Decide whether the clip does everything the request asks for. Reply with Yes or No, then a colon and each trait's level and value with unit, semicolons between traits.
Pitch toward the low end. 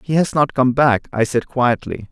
Yes: low, 130 Hz